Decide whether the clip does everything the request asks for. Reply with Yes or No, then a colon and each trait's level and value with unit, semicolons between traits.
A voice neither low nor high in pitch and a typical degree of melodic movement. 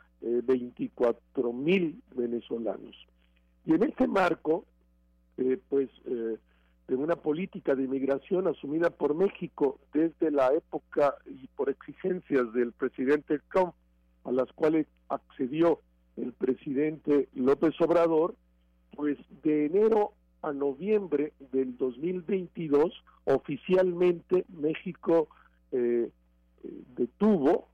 No: medium, 145 Hz; wide, 6.1 semitones